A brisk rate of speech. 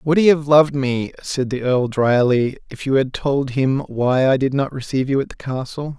Yes: fast, 230 wpm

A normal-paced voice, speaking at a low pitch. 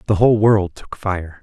No: fast, 210 wpm; low, 100 Hz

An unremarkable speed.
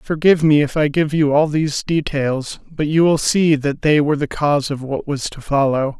No: fast, 230 wpm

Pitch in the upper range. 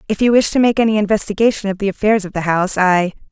Yes: high, 205 Hz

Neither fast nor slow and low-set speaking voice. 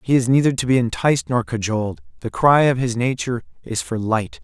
No: fast, 215 wpm; low, 120 Hz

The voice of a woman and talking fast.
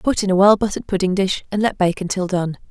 Yes: female; fast, 265 wpm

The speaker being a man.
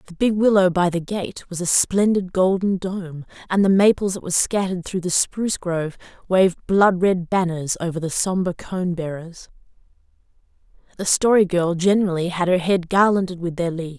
No: female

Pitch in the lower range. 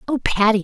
No: high, 220 Hz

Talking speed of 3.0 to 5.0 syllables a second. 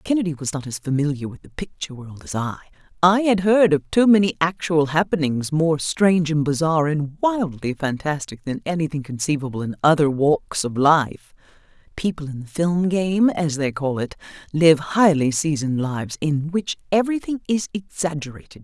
No: 5.2 syllables/s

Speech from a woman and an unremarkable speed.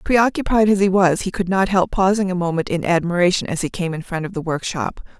No: female; fast, 240 wpm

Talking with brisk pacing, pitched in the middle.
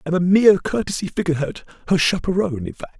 No: average, 180 wpm; medium, 170 Hz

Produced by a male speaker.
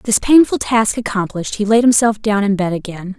No: female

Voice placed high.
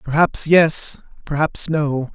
No: medium, 150 Hz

